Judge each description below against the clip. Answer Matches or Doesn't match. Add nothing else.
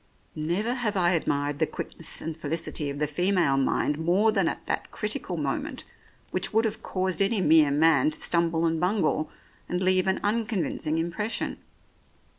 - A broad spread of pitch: Doesn't match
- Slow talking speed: Doesn't match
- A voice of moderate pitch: Matches